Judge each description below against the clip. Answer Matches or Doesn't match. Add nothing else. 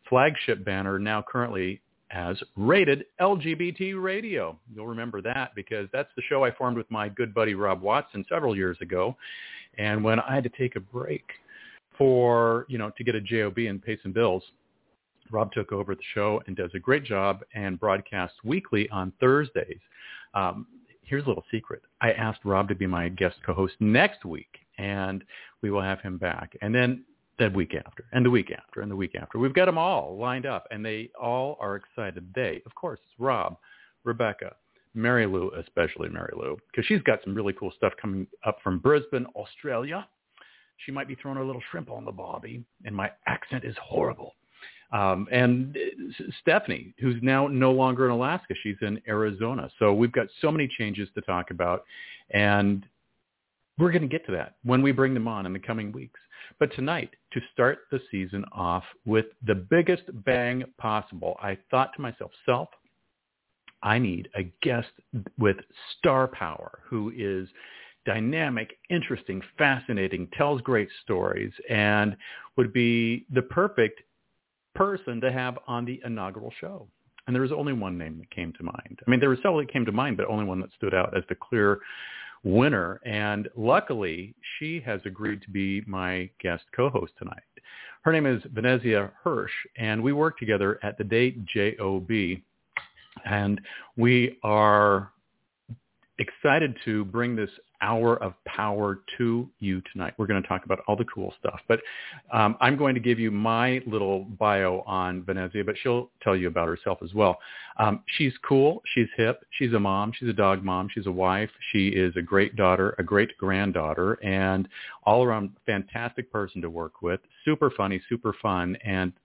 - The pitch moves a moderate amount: Matches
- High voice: Doesn't match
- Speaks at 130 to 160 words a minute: Doesn't match